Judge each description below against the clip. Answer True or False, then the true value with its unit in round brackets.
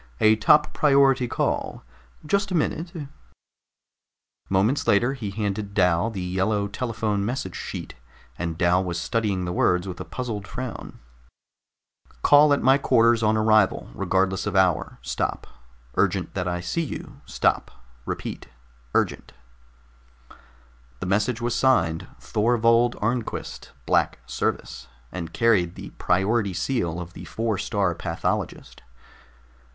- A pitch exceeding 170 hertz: False (105 Hz)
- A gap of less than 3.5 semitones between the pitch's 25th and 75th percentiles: False (4.6 semitones)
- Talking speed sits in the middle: False (130 wpm)